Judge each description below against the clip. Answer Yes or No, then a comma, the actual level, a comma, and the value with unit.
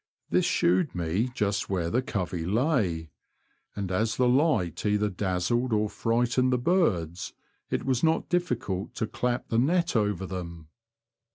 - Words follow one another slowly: No, average, 150 wpm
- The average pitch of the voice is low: Yes, low, 105 Hz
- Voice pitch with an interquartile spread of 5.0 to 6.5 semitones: Yes, wide, 5.6 semitones